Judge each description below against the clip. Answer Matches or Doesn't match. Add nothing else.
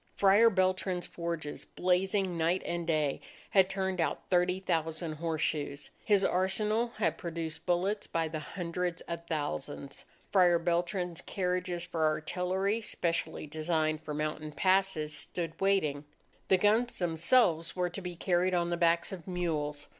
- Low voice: Doesn't match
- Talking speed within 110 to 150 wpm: Matches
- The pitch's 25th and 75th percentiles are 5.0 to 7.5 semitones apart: Doesn't match